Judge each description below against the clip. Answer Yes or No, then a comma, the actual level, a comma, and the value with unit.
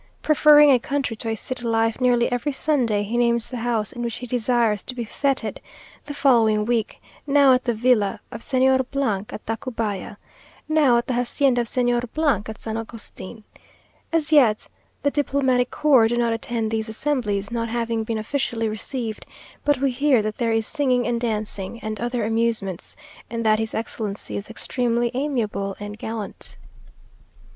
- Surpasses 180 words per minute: No, average, 170 wpm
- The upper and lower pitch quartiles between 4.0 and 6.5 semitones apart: No, narrow, 2.6 semitones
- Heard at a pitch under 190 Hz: No, high, 235 Hz